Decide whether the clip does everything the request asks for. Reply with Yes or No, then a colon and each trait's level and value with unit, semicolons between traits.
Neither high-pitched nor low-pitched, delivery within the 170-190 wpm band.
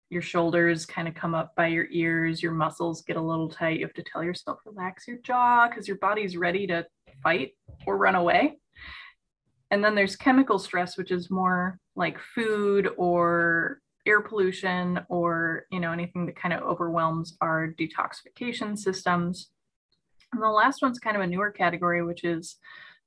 Yes: medium, 180 Hz; average, 175 wpm